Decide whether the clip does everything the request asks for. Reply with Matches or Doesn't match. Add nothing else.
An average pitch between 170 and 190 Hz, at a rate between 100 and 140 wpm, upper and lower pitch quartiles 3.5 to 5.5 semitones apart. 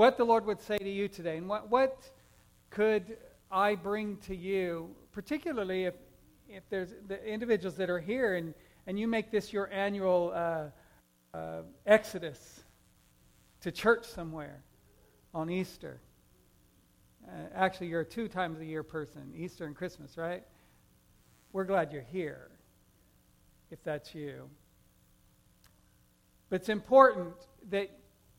Matches